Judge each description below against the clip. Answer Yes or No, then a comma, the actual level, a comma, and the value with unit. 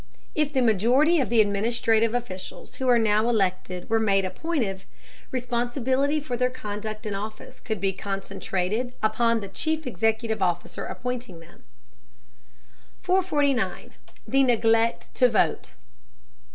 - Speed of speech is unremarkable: No, slow, 125 wpm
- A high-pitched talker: Yes, high, 225 Hz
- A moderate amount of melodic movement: Yes, average, 3.6 semitones